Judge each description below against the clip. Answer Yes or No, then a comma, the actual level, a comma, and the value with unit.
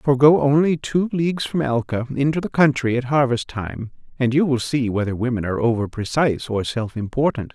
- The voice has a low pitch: Yes, low, 130 Hz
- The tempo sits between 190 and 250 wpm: Yes, average, 200 wpm